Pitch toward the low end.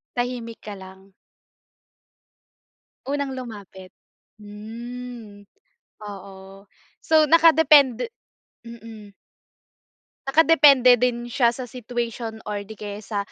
No: high, 235 Hz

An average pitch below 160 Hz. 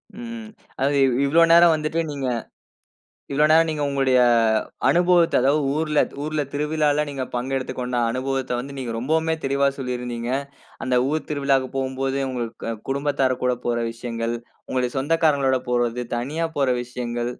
Yes: low, 135 Hz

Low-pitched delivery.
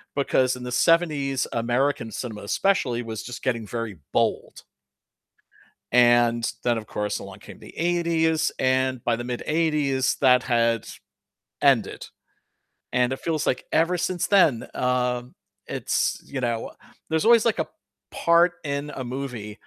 Yes: low, 130 Hz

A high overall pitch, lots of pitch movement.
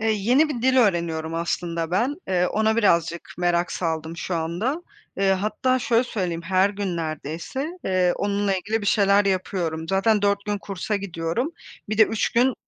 No: high, 195 Hz; average, 4.4 semitones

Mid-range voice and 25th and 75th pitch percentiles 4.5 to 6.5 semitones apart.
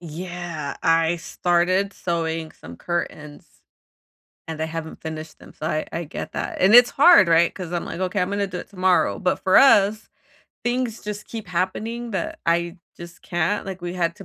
No: medium, 175 Hz; average, 3.1 semitones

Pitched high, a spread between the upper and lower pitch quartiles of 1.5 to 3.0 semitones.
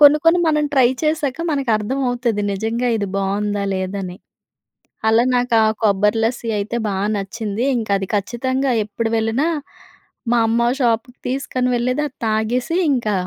No: high, 230 Hz; average, 3.5 semitones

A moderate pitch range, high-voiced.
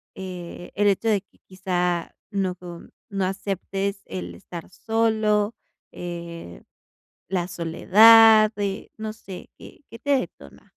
Yes: average, 3.3 semitones; high, 195 Hz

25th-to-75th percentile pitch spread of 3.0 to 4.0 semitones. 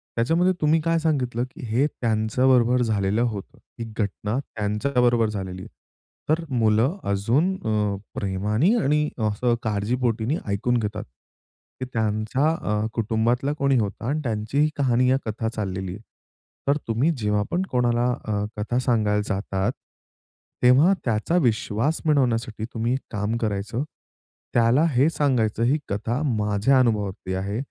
Yes: average, 3.6 semitones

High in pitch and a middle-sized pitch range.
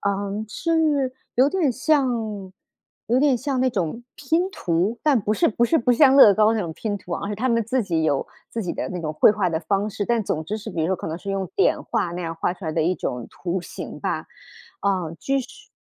No: high, 210 Hz; wide, 6.2 semitones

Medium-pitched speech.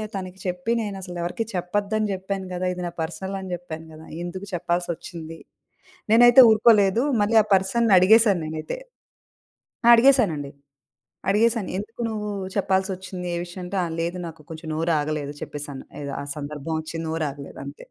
Yes: medium, 180 Hz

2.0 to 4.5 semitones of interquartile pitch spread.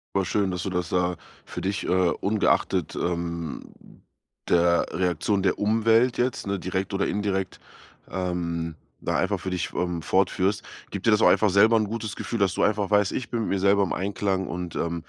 Yes: narrow, 2.6 semitones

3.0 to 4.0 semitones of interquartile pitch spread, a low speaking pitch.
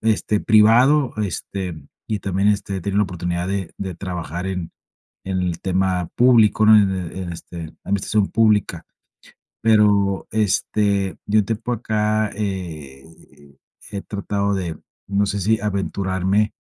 No: narrow, 2.4 semitones; low, 100 Hz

